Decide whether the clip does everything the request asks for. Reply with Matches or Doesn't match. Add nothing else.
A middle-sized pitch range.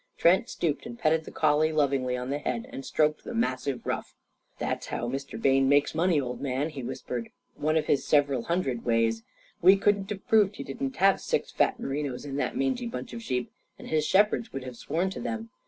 Doesn't match